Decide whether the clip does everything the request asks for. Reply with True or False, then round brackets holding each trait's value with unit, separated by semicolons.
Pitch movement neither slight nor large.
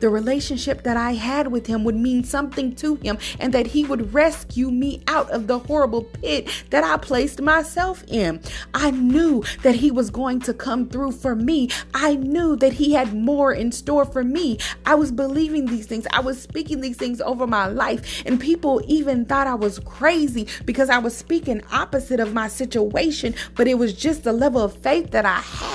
True (3.3 semitones)